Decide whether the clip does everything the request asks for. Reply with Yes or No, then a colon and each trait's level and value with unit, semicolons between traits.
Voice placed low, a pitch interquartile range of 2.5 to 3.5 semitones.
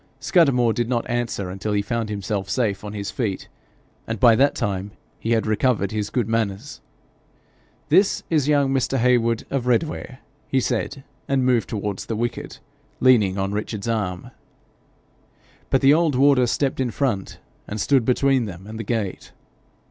No: low, 115 Hz; average, 4.0 semitones